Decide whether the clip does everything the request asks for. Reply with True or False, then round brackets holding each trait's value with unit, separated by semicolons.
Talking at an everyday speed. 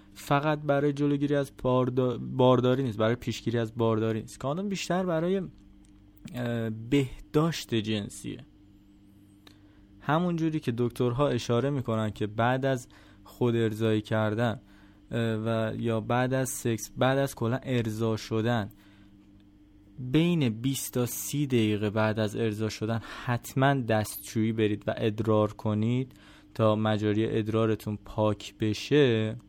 True (120 wpm)